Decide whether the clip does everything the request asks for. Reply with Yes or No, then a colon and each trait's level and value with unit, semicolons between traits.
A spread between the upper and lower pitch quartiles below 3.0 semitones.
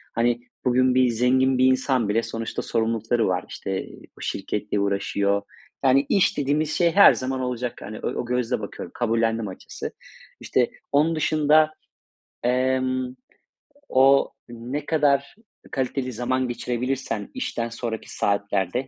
Yes: narrow, 2.6 semitones